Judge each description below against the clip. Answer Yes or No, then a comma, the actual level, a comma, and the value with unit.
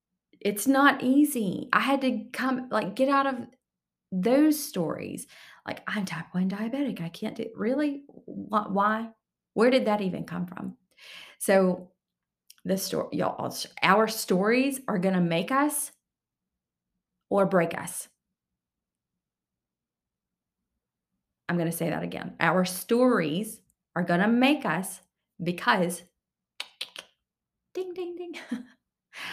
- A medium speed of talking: No, slow, 115 wpm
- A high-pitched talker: Yes, high, 215 Hz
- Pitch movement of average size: No, wide, 6.1 semitones